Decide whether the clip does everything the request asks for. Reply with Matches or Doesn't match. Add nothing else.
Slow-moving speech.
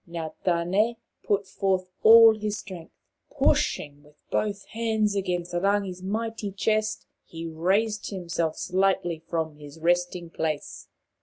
Matches